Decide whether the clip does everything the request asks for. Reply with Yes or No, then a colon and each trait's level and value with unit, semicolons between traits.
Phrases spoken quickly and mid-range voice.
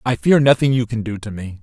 No: fast, 295 wpm; low, 115 Hz